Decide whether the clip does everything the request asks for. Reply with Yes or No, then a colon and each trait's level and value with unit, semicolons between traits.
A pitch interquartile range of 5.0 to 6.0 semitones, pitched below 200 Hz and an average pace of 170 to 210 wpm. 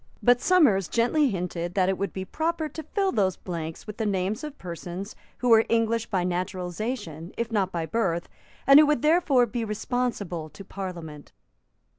No: wide, 5.4 semitones; high, 205 Hz; average, 175 wpm